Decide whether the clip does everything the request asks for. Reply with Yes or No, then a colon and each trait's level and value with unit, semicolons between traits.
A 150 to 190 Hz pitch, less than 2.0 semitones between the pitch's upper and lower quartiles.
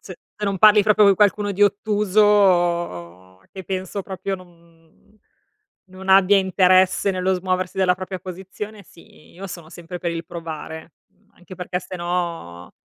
No: medium, 185 Hz; narrow, 2.4 semitones